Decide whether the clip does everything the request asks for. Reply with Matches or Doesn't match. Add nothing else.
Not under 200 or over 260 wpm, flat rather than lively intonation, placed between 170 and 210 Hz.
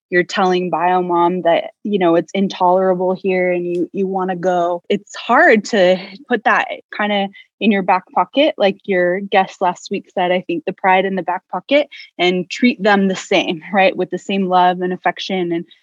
Matches